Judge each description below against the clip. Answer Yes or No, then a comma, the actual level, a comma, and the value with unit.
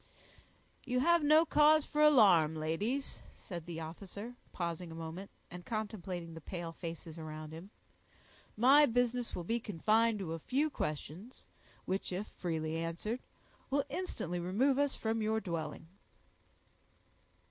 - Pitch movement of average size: No, wide, 6.9 semitones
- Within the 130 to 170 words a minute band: Yes, slow, 135 wpm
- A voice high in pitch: Yes, high, 195 Hz